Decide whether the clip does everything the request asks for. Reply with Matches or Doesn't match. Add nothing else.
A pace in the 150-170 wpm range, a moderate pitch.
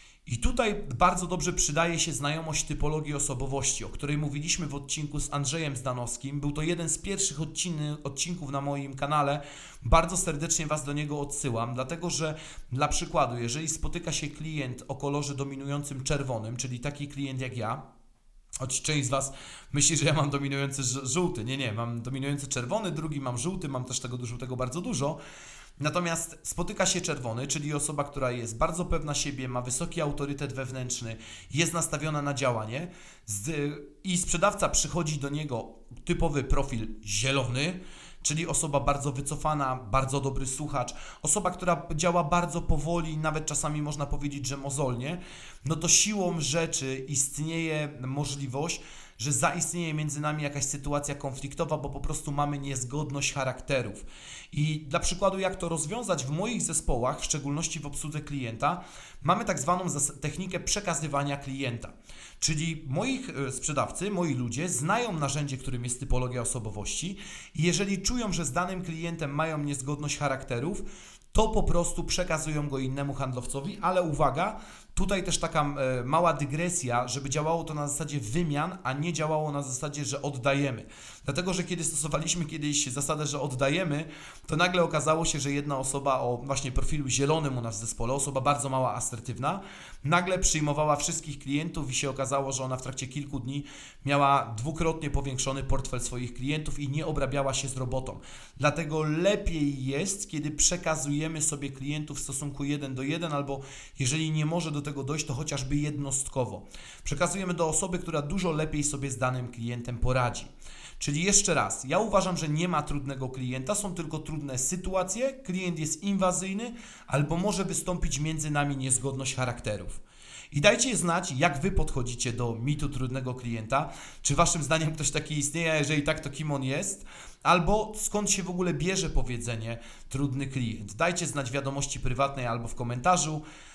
Matches